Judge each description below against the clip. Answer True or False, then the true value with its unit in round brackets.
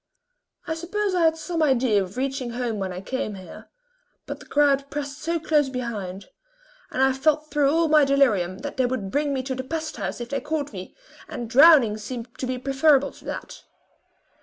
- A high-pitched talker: True (270 Hz)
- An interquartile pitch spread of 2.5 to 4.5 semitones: True (4.1 semitones)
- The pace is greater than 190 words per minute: True (200 wpm)